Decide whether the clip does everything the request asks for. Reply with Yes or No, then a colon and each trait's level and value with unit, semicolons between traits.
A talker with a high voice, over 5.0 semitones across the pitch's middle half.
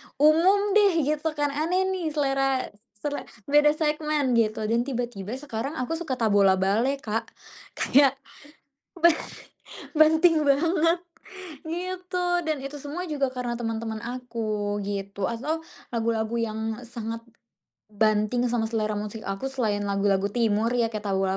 Yes: very high, 250 Hz; wide, 5.6 semitones